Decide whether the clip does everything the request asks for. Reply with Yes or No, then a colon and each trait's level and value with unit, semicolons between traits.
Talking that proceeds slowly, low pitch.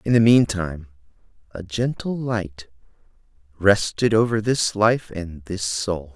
Yes: slow, 125 wpm; low, 100 Hz